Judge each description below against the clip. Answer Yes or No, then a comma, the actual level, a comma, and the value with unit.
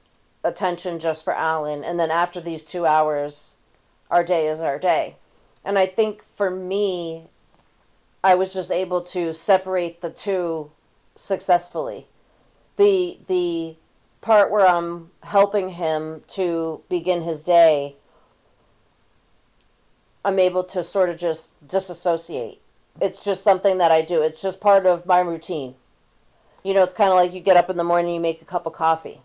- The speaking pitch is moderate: Yes, medium, 175 Hz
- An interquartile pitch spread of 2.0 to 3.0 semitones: Yes, narrow, 2.5 semitones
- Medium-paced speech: Yes, average, 160 wpm